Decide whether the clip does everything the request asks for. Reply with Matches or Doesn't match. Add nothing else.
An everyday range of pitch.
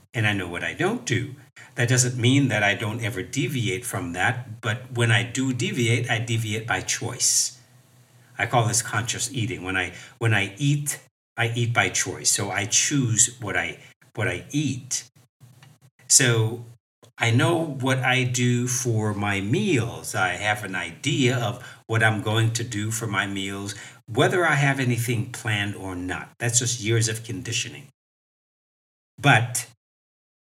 Doesn't match